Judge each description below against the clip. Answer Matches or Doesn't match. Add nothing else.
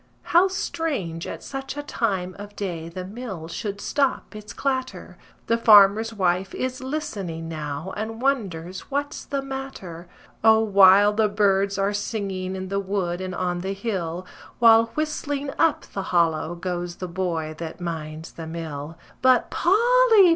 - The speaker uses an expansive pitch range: Matches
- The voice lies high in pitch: Matches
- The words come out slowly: Doesn't match